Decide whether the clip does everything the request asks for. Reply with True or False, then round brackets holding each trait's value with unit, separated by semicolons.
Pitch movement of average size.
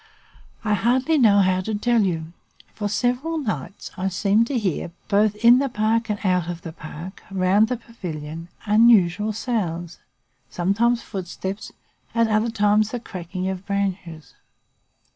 True (3.9 semitones)